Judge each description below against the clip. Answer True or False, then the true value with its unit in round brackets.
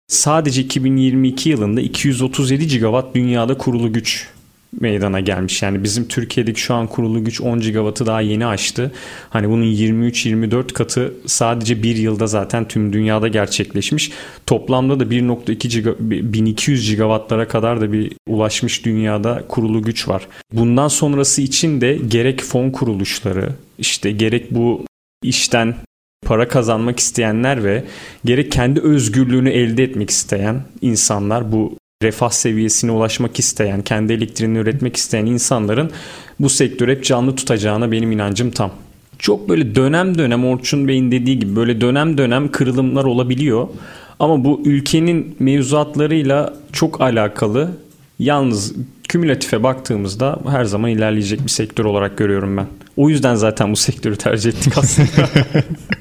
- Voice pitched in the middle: False (120 Hz)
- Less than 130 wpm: False (135 wpm)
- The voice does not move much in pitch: False (3.5 semitones)